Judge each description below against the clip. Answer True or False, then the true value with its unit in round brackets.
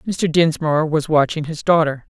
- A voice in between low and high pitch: True (155 Hz)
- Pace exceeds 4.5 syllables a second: True (4.9 syllables/s)